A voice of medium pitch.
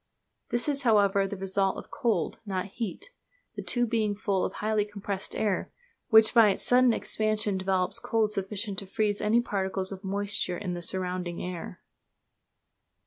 No: high, 205 Hz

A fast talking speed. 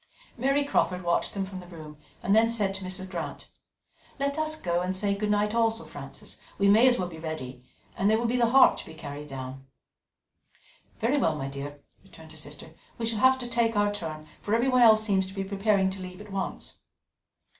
Yes: fast, 215 wpm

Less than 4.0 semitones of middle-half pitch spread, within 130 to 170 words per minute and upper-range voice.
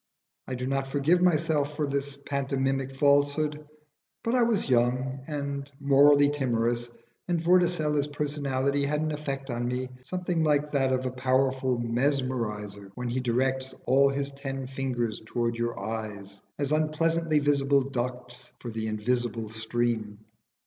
No: average, 3.0 semitones; average, 140 wpm; low, 135 Hz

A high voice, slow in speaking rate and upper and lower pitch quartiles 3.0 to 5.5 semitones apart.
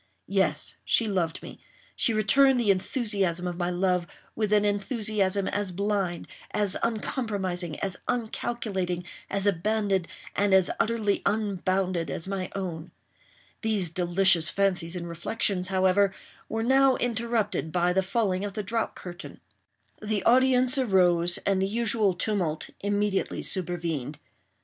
Yes: high, 195 Hz; slow, 120 wpm; average, 3.3 semitones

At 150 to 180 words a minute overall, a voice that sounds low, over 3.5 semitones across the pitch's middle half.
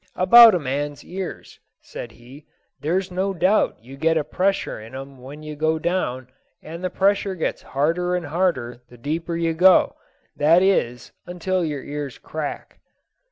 No: average, 160 wpm; medium, 160 Hz; average, 4.6 semitones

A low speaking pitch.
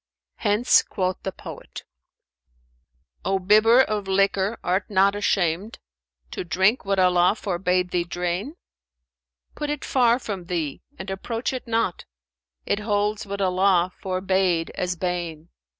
No: high, 190 Hz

